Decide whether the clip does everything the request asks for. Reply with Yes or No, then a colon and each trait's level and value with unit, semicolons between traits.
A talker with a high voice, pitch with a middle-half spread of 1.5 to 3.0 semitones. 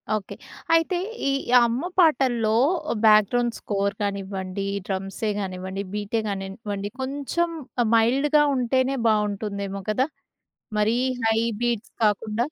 No: high, 215 Hz; average, 3.5 semitones